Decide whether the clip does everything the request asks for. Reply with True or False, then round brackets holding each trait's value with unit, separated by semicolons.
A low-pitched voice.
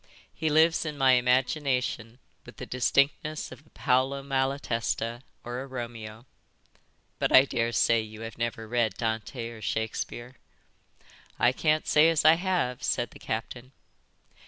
True (125 Hz)